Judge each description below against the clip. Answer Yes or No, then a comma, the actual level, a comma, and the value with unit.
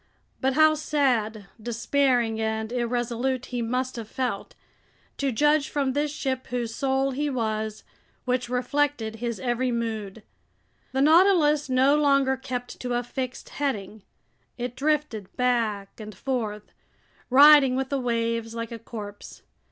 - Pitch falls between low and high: No, very high, 250 Hz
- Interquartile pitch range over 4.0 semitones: No, average, 3.2 semitones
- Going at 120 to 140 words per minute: Yes, slow, 135 wpm